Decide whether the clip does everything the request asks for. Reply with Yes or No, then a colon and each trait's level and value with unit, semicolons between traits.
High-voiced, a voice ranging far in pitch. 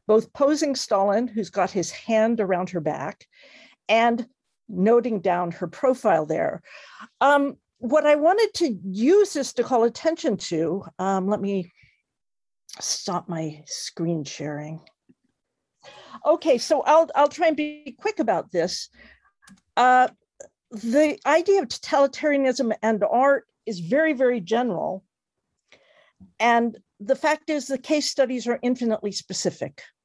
Yes: high, 235 Hz; wide, 6.8 semitones